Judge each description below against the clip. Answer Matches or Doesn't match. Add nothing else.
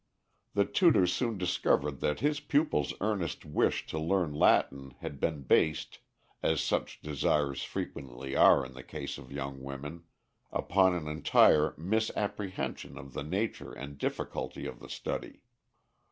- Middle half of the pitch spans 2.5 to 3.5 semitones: Doesn't match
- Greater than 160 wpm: Doesn't match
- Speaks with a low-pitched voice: Matches